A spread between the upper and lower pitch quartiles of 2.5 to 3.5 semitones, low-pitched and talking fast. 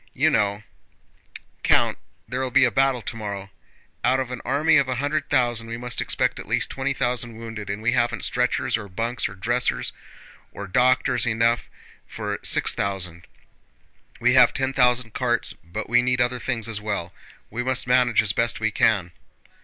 No: average, 2.8 semitones; low, 120 Hz; average, 170 wpm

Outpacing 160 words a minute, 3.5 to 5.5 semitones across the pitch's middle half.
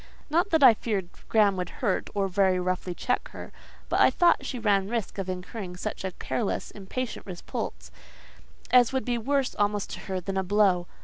Yes: average, 190 wpm; average, 4.5 semitones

